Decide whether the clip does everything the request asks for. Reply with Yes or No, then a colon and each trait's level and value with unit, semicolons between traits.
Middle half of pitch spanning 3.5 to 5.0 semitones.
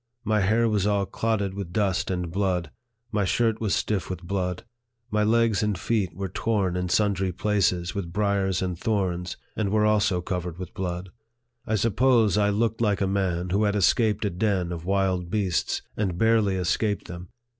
No: average, 2.8 semitones